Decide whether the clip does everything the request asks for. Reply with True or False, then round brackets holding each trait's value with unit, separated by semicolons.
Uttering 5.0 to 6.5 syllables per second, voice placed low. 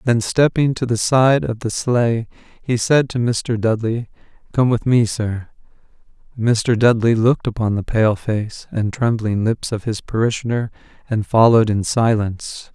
False (4.4 syllables/s; 115 Hz)